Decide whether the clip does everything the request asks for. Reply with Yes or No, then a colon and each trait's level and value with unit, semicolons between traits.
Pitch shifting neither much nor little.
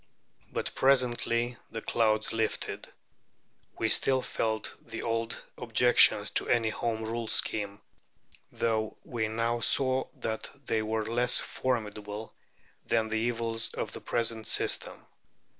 No: narrow, 1.3 semitones